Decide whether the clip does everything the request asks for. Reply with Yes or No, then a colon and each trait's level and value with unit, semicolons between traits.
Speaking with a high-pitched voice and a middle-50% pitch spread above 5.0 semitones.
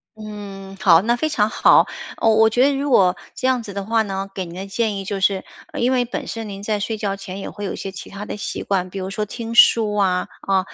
No: high, 205 Hz; narrow, 2.5 semitones